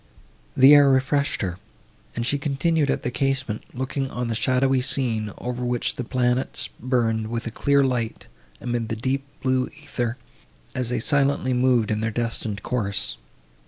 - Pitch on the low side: Yes, low, 125 Hz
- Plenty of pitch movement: No, average, 2.7 semitones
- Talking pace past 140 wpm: Yes, average, 160 wpm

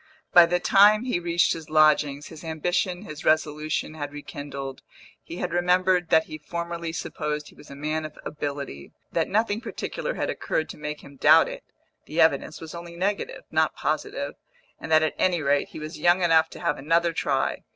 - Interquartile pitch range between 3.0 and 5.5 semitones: No, narrow, 2.6 semitones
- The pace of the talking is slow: No, average, 190 wpm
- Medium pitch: Yes, medium, 160 Hz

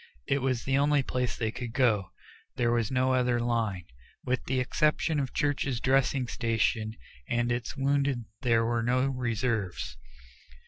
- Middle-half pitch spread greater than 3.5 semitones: No, narrow, 2.5 semitones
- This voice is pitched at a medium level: No, low, 125 Hz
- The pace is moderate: Yes, average, 150 wpm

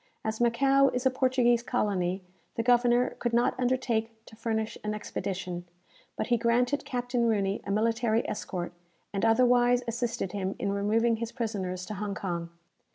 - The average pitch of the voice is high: Yes, high, 230 Hz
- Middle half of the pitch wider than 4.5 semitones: No, average, 3.3 semitones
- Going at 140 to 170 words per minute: Yes, average, 160 wpm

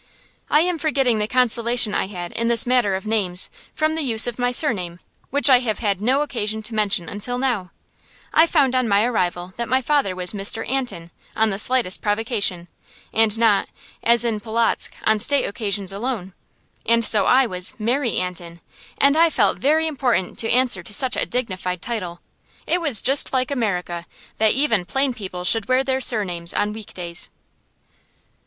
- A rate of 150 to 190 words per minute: Yes, average, 180 wpm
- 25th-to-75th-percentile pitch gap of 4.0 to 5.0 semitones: Yes, average, 4.7 semitones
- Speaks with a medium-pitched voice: No, high, 225 Hz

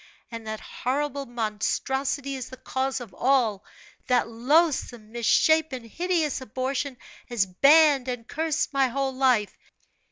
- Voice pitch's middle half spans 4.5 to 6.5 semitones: No, average, 3.1 semitones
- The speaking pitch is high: Yes, very high, 260 Hz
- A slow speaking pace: Yes, slow, 125 wpm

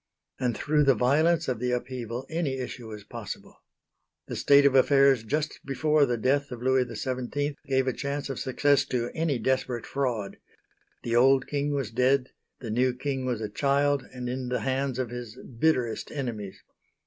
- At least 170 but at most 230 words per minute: Yes, average, 175 wpm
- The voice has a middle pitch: No, low, 130 Hz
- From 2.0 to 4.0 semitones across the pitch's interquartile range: Yes, narrow, 2.4 semitones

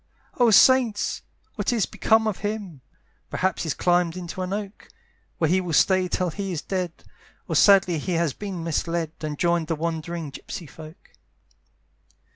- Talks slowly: No, average, 160 wpm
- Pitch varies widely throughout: No, average, 3.2 semitones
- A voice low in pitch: No, medium, 175 Hz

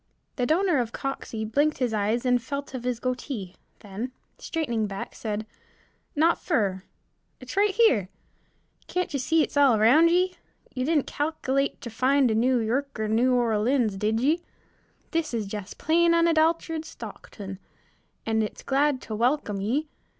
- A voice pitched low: No, very high, 255 Hz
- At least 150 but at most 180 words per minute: Yes, average, 155 wpm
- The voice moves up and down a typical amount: No, wide, 5.7 semitones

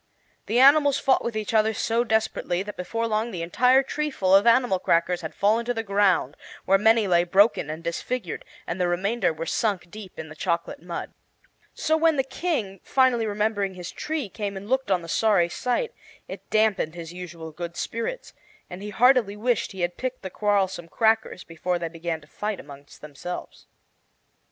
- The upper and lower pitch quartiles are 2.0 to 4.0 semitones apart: No, average, 4.8 semitones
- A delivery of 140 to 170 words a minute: No, average, 185 wpm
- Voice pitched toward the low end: No, high, 200 Hz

